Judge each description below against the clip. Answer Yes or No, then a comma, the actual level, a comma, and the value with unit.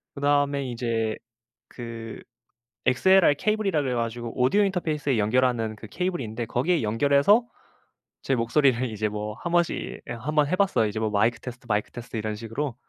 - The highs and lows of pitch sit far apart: No, average, 4.8 semitones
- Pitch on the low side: Yes, low, 125 Hz